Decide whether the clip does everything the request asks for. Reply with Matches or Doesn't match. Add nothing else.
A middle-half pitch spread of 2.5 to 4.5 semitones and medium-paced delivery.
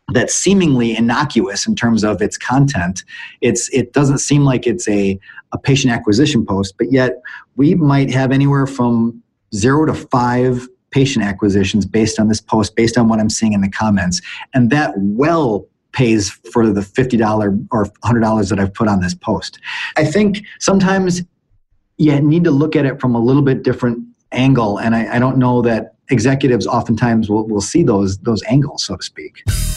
Matches